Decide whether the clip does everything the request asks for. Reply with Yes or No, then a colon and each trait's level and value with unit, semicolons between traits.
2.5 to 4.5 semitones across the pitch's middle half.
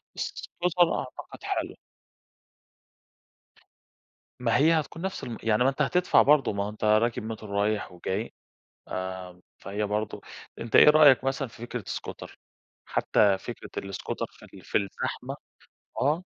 No: average, 5.1 semitones